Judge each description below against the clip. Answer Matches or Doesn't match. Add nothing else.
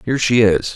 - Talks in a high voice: Doesn't match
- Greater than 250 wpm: Doesn't match